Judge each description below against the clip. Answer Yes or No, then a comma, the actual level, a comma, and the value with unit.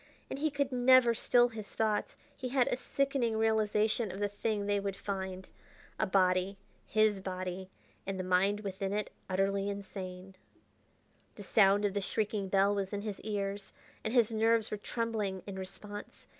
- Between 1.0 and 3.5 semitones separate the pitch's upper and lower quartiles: Yes, narrow, 2.4 semitones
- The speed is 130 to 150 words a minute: No, average, 170 wpm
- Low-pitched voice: No, high, 205 Hz